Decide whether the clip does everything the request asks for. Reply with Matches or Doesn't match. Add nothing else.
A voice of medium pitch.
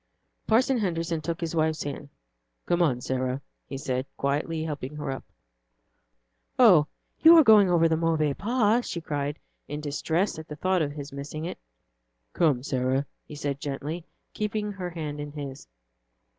Matches